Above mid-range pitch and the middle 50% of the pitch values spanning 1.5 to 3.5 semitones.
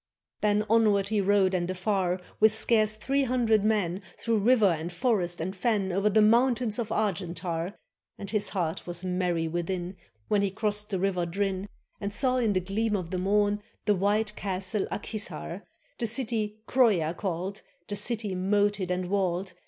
Yes: high, 200 Hz; average, 2.8 semitones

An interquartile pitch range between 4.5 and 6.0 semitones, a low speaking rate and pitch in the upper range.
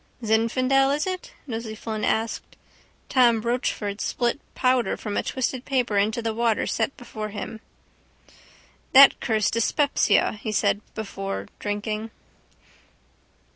No: average, 2.9 semitones; slow, 120 wpm; high, 225 Hz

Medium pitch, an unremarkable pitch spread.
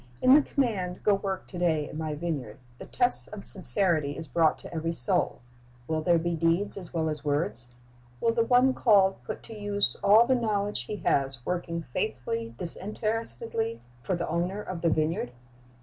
Yes: medium, 175 Hz; average, 4.9 semitones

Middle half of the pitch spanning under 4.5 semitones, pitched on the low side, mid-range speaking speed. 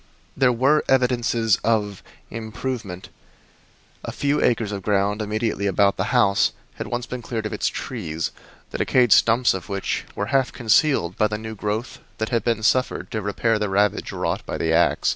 Yes: average, 3.1 semitones; low, 110 Hz; average, 180 wpm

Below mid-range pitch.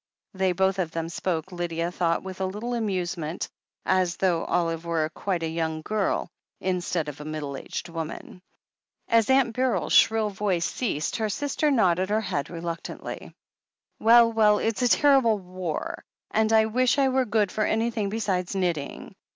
No: high, 190 Hz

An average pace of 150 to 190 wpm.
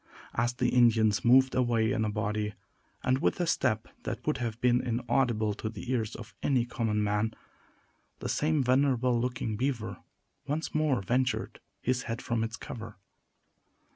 Yes: average, 160 wpm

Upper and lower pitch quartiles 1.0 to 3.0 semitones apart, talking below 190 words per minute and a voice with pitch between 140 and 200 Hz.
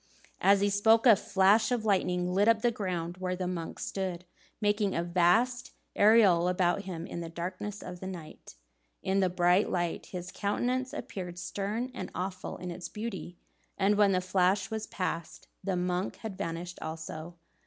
Yes: average, 2.7 semitones; average, 175 wpm; medium, 185 Hz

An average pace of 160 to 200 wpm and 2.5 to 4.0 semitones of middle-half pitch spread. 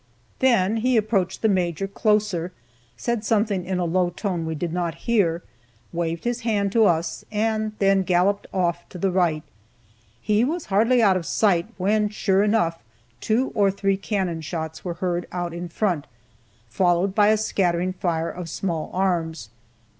Yes: average, 165 wpm; average, 3.6 semitones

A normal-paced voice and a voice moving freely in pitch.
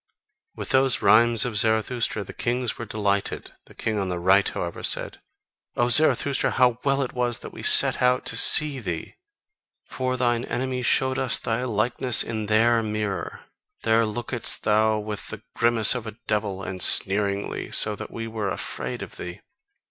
No: average, 170 wpm; average, 2.9 semitones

